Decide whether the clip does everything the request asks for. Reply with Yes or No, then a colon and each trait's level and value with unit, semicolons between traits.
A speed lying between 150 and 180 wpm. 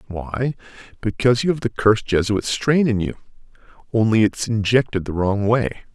Yes: average, 160 wpm